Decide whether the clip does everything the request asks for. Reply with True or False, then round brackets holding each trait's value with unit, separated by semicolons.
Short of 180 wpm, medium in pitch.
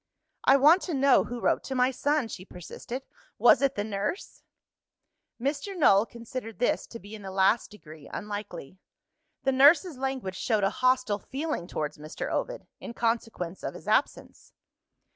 False (160 wpm; 235 Hz)